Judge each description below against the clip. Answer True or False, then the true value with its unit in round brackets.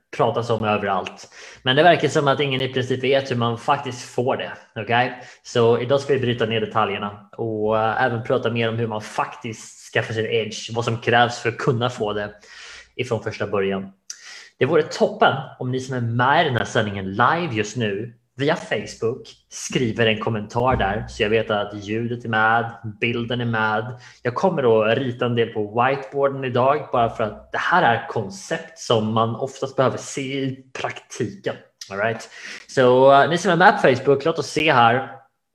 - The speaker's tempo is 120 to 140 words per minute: False (195 wpm)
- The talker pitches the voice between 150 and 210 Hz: False (120 Hz)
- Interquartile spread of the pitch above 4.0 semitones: False (3.3 semitones)